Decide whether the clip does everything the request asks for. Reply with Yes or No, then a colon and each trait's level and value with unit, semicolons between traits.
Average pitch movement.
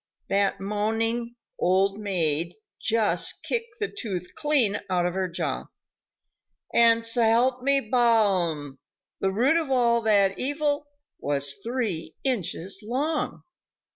Yes: average, 4.9 semitones